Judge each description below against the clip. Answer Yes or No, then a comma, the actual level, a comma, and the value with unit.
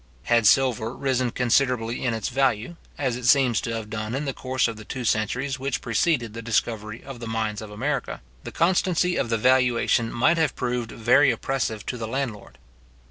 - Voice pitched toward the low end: Yes, low, 120 Hz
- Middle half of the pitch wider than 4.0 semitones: No, average, 3.0 semitones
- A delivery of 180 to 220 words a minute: Yes, average, 190 wpm